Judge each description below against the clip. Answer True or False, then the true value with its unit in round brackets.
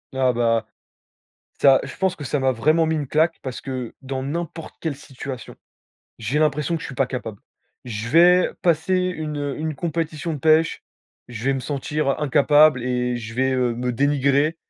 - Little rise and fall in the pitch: False (3.6 semitones)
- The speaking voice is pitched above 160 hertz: False (140 Hz)